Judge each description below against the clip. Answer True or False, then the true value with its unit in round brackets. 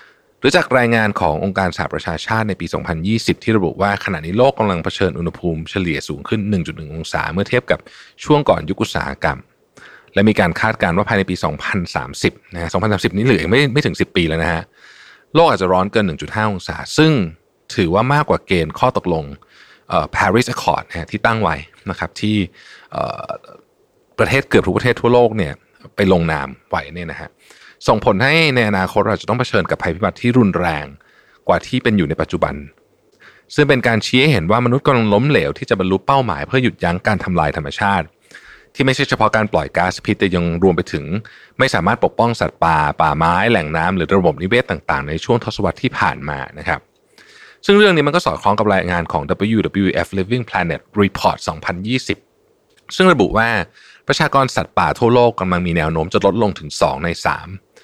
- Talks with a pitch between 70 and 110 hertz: True (100 Hz)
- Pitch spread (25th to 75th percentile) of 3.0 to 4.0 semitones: False (5.5 semitones)